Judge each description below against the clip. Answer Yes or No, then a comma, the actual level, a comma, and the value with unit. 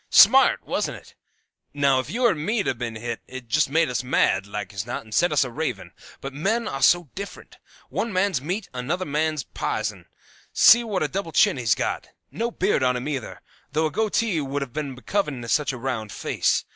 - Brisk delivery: Yes, fast, 210 wpm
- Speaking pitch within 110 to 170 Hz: Yes, medium, 140 Hz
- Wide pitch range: Yes, wide, 6.4 semitones